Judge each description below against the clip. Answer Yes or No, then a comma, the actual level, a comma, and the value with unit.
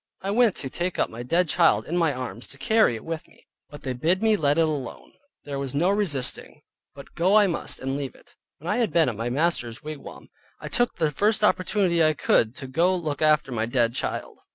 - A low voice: No, medium, 155 Hz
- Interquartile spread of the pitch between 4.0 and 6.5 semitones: Yes, wide, 5.4 semitones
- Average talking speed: No, fast, 235 wpm